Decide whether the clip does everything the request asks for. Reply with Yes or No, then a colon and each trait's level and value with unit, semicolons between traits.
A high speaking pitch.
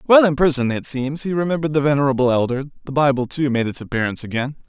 No: medium, 140 Hz